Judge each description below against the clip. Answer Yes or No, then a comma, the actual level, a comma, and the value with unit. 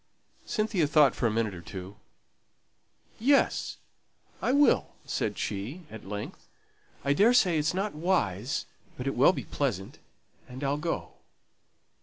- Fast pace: No, slow, 135 wpm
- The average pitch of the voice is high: No, medium, 140 Hz